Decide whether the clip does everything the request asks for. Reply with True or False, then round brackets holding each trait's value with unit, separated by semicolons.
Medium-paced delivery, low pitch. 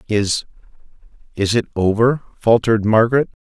False (85 wpm; 110 Hz)